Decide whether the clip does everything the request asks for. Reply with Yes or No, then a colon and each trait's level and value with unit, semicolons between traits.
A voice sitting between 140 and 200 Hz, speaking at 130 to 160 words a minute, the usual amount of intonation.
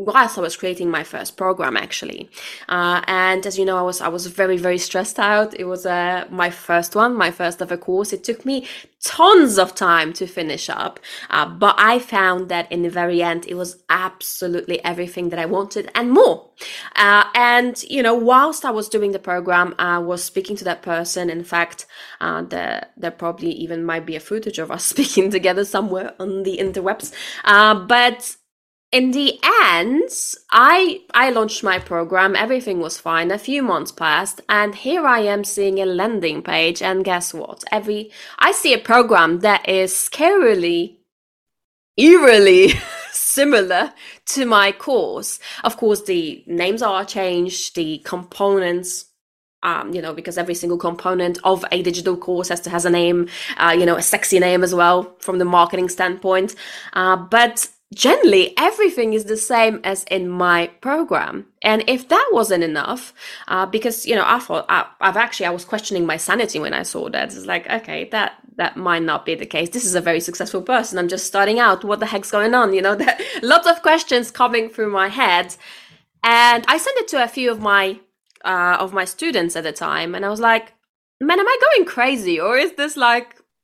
No: high, 190 Hz; average, 195 wpm; average, 4.8 semitones